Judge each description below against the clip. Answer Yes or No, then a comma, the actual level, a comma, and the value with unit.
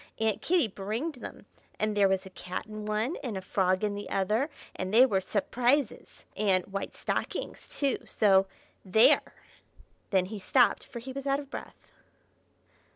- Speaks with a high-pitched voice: Yes, high, 215 Hz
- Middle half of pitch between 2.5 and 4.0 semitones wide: No, average, 4.5 semitones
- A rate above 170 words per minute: No, average, 165 wpm